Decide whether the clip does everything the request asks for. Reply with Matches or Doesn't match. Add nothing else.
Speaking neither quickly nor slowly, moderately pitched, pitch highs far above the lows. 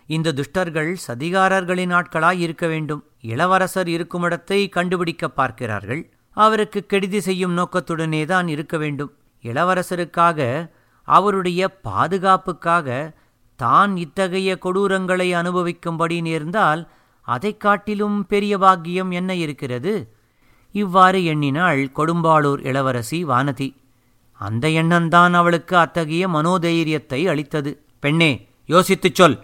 Doesn't match